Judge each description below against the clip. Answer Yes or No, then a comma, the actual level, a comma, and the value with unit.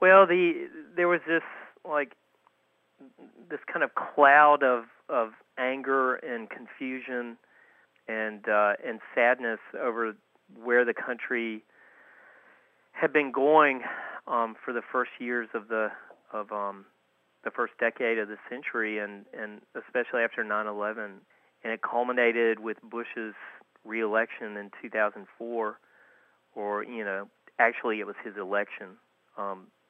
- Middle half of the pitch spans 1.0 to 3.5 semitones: No, average, 4.5 semitones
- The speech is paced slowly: Yes, slow, 125 wpm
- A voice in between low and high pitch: No, low, 120 Hz